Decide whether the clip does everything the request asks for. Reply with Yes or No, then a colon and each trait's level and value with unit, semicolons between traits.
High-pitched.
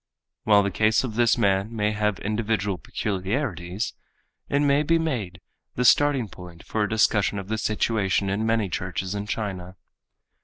No: low, 105 Hz